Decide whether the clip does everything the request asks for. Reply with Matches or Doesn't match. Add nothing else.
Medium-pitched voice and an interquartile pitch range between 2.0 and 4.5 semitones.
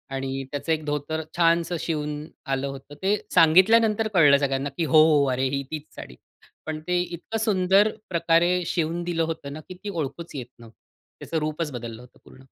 Matches